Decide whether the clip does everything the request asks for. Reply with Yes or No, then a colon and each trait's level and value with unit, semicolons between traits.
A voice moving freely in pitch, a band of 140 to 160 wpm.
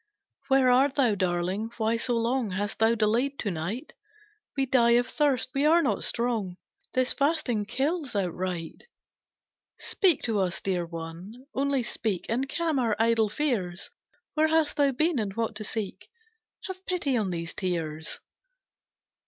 Yes: wide, 5.9 semitones; average, 155 wpm